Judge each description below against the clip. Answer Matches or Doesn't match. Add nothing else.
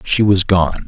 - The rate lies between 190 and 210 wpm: Matches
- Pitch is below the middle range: Matches